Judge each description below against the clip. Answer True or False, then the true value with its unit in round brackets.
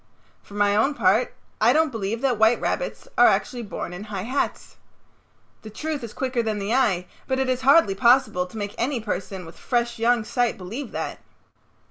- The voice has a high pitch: True (230 Hz)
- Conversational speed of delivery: True (190 wpm)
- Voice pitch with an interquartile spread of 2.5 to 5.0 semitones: True (4.1 semitones)